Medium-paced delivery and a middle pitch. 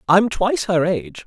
Yes: average, 190 wpm; medium, 170 Hz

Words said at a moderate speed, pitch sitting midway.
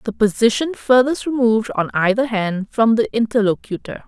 No: average, 145 wpm; high, 225 Hz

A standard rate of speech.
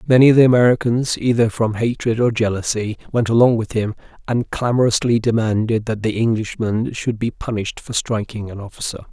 Yes: average, 170 wpm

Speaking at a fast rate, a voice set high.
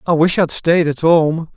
No: fast, 270 wpm; medium, 165 Hz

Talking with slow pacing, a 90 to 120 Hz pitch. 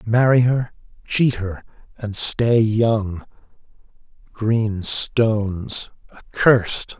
Yes: slow, 85 wpm; low, 110 Hz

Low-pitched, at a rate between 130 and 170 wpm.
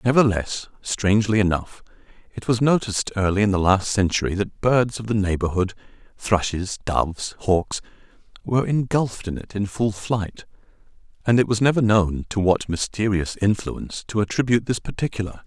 Yes: low, 105 Hz; average, 145 wpm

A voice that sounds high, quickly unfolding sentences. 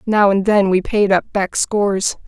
Yes: high, 200 Hz; fast, 210 wpm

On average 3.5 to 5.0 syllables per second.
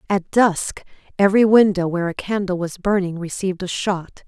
No: 5.4 syllables/s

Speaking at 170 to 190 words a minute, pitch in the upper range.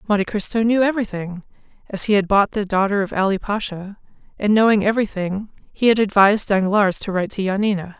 Yes: average, 180 wpm; high, 205 Hz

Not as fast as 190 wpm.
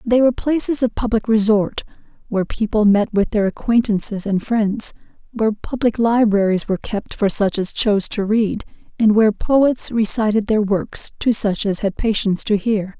Yes: average, 175 wpm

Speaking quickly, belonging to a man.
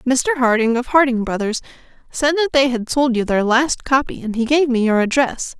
No: fast, 215 wpm; female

